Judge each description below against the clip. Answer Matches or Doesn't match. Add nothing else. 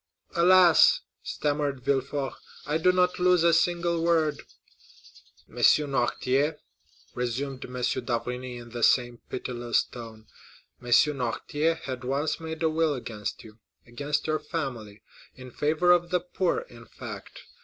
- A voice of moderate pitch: Matches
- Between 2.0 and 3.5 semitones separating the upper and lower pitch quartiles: Doesn't match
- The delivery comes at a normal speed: Doesn't match